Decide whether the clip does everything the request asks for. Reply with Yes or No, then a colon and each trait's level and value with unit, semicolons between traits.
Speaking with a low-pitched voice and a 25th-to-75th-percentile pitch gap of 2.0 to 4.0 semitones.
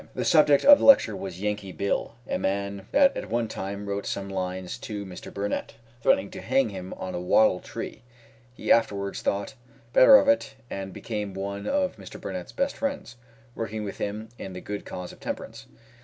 Yes: low, 100 Hz; average, 3.2 semitones